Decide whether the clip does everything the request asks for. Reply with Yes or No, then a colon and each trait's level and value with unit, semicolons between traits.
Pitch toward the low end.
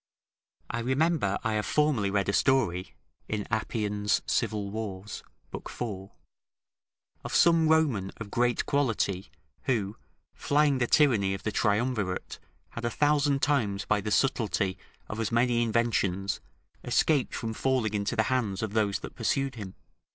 Yes: low, 110 Hz